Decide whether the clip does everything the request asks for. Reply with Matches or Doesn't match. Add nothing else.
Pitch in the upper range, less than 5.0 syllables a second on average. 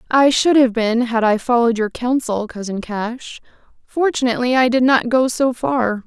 Matches